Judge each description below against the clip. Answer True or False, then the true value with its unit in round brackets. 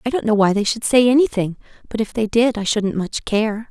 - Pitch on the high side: True (220 Hz)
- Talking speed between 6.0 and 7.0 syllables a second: False (5.5 syllables/s)